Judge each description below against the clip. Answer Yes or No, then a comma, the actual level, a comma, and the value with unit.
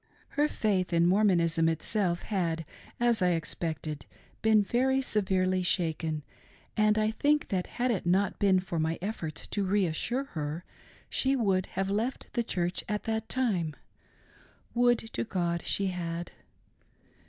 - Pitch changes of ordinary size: Yes, average, 4.4 semitones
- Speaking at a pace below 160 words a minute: Yes, average, 145 wpm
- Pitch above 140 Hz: Yes, high, 190 Hz